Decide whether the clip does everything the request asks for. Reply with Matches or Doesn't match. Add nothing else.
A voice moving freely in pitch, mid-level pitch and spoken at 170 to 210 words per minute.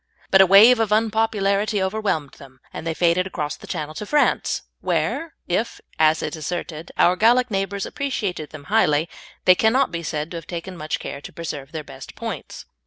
Matches